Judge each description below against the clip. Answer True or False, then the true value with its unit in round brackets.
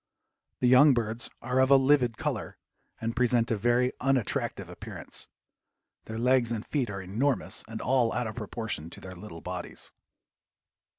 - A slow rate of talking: False (160 wpm)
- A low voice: True (120 Hz)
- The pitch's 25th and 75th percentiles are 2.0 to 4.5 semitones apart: True (2.9 semitones)